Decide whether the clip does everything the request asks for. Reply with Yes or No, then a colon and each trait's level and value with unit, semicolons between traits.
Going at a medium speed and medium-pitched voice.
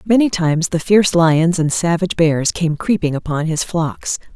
Yes: average, 180 wpm; medium, 170 Hz